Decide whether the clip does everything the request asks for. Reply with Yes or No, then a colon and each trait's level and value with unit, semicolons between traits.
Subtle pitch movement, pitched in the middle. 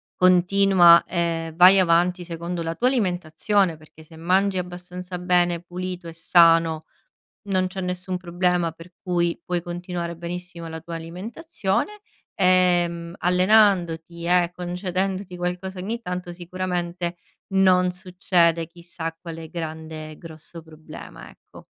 Yes: narrow, 1.5 semitones; medium, 175 Hz